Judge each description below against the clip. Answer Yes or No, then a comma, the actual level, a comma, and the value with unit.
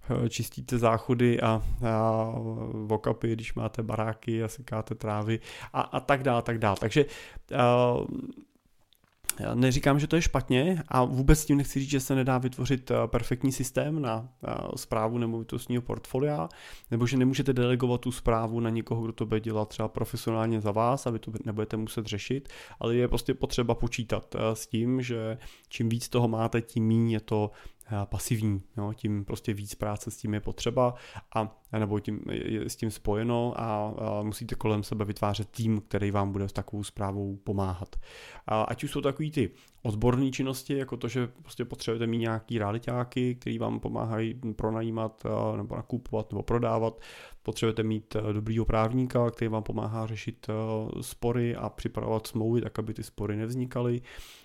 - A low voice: Yes, low, 115 Hz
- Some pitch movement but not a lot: No, narrow, 2.0 semitones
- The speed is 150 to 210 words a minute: Yes, average, 165 wpm